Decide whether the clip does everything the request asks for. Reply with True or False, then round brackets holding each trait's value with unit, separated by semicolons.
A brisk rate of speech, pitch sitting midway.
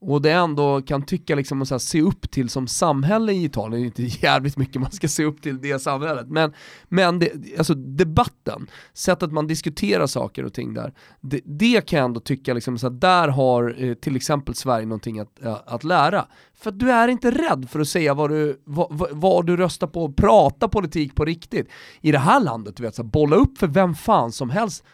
True (215 wpm; 150 Hz)